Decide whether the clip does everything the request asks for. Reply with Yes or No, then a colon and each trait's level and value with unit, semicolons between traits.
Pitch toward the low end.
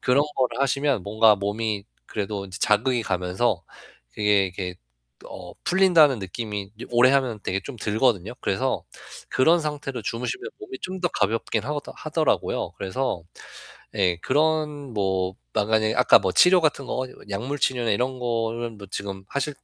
Yes: low, 115 Hz